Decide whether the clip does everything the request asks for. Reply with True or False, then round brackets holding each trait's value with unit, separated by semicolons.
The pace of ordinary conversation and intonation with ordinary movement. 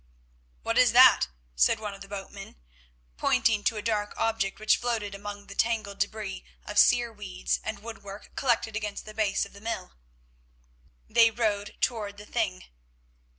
False (160 wpm; 2.0 semitones)